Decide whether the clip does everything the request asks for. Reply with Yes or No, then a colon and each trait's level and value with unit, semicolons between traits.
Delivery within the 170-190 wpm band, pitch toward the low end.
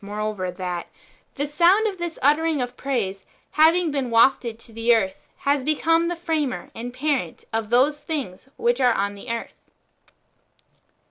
No: average, 175 wpm; very high, 255 Hz